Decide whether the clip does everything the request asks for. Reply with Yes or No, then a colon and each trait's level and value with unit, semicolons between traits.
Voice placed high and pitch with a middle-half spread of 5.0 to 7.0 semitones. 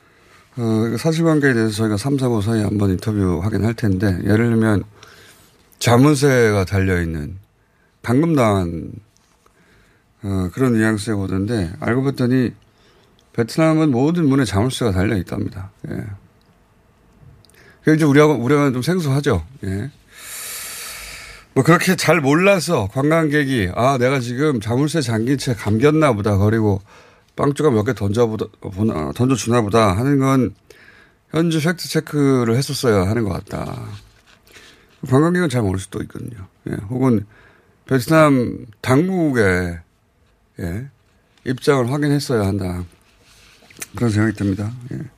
No: low, 115 Hz; wide, 5.6 semitones